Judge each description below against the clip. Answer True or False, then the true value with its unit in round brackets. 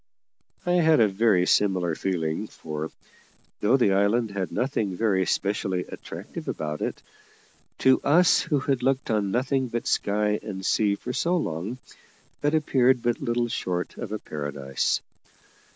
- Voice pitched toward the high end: False (105 Hz)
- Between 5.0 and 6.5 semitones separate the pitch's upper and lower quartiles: True (5.6 semitones)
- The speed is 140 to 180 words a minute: True (150 wpm)